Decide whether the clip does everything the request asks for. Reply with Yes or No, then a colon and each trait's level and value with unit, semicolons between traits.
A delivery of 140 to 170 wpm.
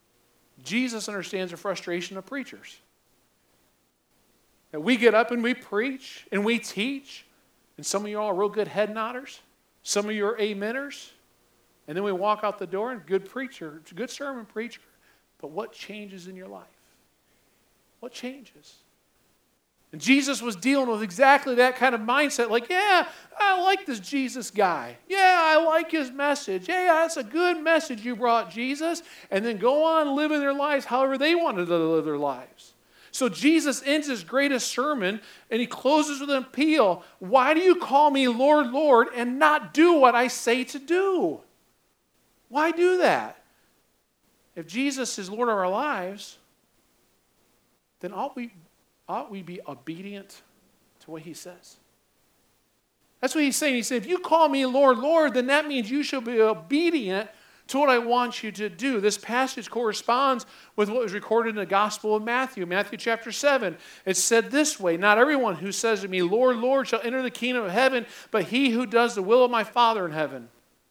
No: average, 180 wpm